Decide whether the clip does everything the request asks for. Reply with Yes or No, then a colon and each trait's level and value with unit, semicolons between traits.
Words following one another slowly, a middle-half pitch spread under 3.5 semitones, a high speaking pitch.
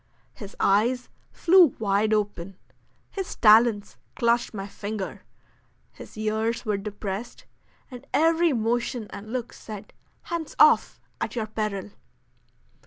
Yes: slow, 115 wpm; average, 3.0 semitones; high, 220 Hz